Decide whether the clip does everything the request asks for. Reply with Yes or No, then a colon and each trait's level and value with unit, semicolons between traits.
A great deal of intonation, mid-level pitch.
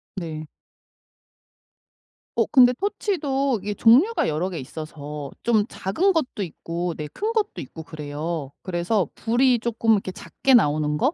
No: wide, 8.5 semitones; high, 195 Hz